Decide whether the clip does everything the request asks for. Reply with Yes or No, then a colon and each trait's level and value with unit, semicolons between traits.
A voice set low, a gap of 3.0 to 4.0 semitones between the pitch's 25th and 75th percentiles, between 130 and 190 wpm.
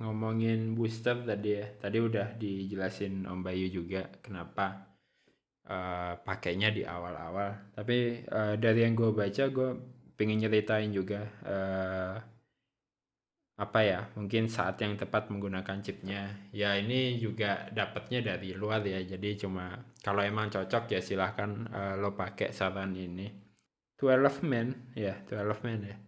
No: low, 105 Hz; narrow, 2.6 semitones; fast, 140 wpm